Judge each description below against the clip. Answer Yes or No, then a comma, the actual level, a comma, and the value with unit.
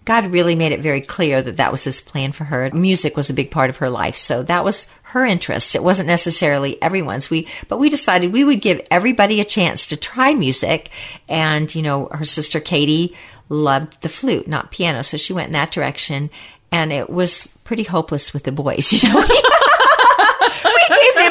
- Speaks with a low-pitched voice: No, medium, 160 Hz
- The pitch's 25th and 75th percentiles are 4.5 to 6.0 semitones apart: Yes, average, 4.8 semitones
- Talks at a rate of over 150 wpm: Yes, fast, 205 wpm